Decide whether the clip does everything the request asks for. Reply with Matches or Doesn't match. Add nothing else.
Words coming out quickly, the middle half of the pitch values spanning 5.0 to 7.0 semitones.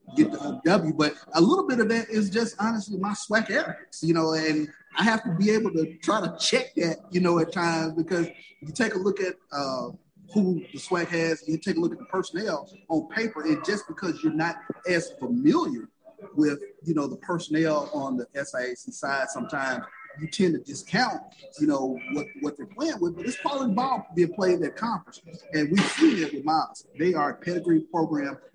Matches